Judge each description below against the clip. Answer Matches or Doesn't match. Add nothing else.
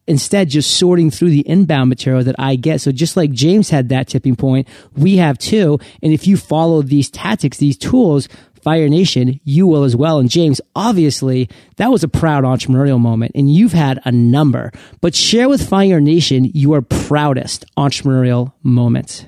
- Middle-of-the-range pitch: Matches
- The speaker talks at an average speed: Matches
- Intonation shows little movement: Doesn't match